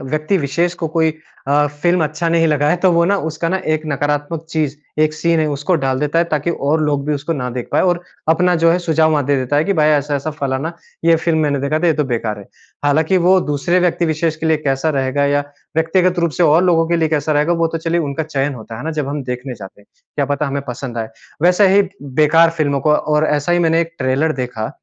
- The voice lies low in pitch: No, medium, 155 Hz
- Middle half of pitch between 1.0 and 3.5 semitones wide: Yes, average, 2.7 semitones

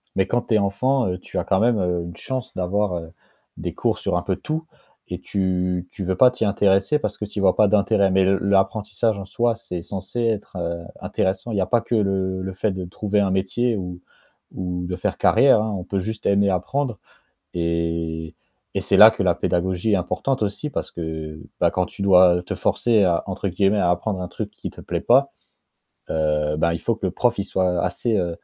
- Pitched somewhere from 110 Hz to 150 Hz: No, very low, 95 Hz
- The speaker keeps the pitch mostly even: No, average, 3.1 semitones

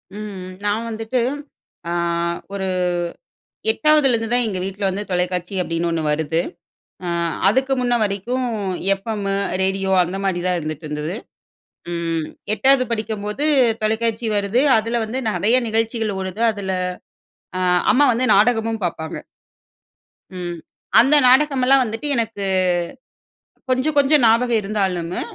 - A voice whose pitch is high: Yes, high, 215 Hz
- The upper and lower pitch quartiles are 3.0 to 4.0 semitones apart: No, average, 4.5 semitones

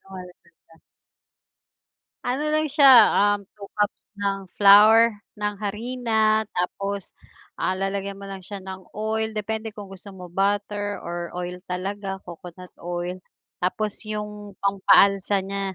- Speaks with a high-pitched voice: Yes, high, 200 Hz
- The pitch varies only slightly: Yes, narrow, 2.0 semitones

